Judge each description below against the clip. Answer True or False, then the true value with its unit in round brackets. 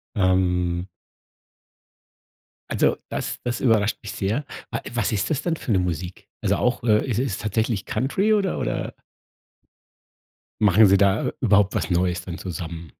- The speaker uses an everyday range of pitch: True (4.5 semitones)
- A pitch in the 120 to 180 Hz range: False (100 Hz)